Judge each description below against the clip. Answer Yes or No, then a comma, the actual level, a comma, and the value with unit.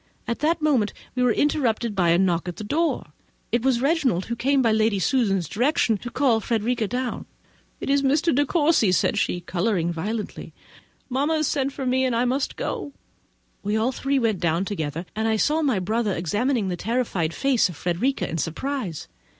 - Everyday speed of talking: Yes, average, 190 wpm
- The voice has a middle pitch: No, high, 235 Hz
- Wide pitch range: Yes, wide, 6.0 semitones